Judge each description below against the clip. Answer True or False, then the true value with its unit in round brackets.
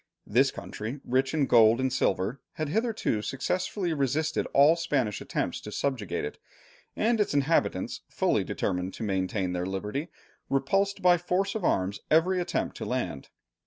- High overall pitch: False (135 Hz)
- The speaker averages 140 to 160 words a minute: True (155 wpm)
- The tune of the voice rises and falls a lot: True (8.2 semitones)